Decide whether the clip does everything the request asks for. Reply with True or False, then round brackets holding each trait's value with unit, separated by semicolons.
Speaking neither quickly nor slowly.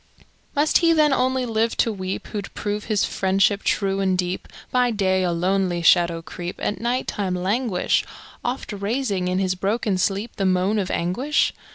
True (175 wpm)